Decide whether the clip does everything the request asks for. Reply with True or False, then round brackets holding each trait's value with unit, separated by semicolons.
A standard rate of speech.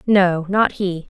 True (150 wpm)